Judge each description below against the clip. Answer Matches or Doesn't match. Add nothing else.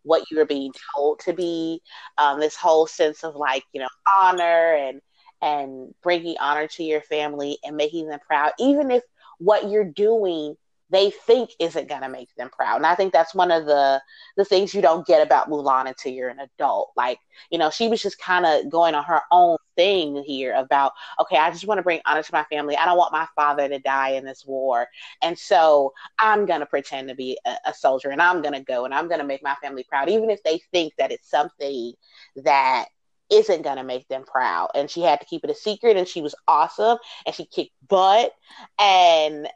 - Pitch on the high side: Doesn't match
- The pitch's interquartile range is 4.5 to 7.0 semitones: Matches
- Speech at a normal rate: Doesn't match